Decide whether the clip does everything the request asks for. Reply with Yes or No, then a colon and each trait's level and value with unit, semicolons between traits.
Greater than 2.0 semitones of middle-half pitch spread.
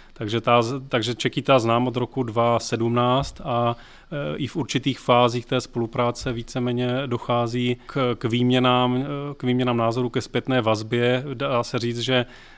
No: narrow, 1.3 semitones